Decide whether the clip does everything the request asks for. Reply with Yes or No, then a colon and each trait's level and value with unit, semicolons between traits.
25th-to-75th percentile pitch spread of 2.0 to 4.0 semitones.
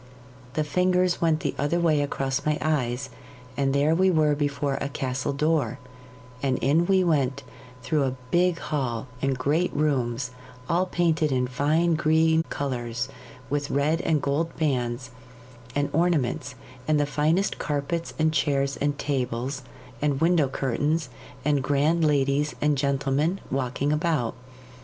Yes: average, 2.8 semitones